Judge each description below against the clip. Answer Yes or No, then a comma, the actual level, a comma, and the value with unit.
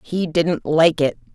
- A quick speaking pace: No, average, 180 wpm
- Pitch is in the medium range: Yes, medium, 155 Hz